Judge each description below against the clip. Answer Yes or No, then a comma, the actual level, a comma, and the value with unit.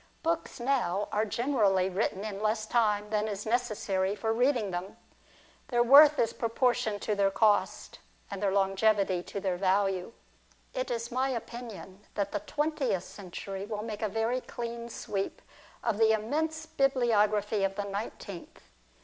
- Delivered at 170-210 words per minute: No, average, 150 wpm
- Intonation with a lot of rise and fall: No, average, 3.3 semitones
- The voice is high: Yes, high, 215 Hz